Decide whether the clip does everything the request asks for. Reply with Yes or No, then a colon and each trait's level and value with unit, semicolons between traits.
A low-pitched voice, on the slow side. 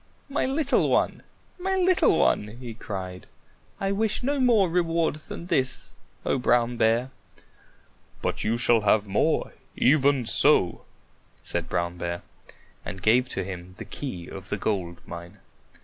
No: low, 120 Hz; average, 145 wpm